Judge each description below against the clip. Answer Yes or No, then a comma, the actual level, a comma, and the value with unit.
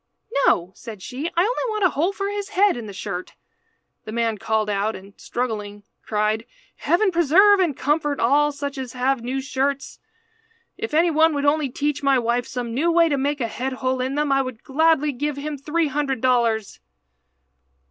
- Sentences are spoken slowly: No, average, 190 wpm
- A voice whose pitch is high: Yes, very high, 275 Hz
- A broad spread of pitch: No, average, 4.7 semitones